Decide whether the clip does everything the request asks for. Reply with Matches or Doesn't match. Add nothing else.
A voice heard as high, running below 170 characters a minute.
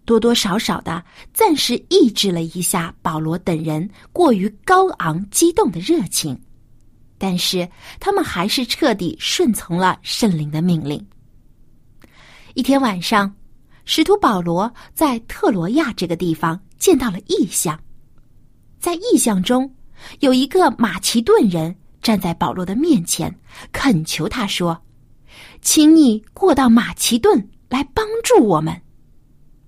Doesn't match